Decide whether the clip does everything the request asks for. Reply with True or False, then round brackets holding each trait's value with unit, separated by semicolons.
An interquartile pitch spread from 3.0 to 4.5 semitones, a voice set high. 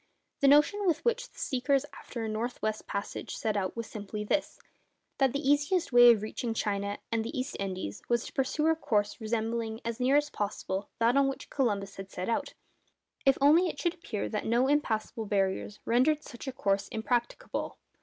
False (4.9 semitones; 235 Hz)